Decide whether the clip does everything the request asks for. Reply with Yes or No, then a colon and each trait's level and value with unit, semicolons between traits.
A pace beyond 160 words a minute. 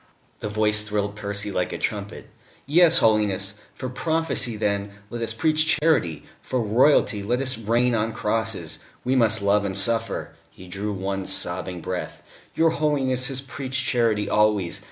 No: average, 155 wpm